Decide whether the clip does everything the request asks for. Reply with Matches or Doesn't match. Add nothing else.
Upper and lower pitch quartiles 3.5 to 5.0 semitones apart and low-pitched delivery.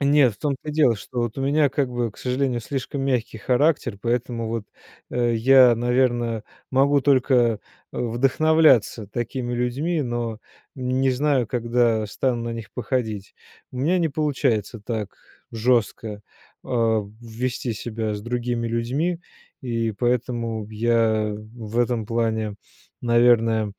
Doesn't match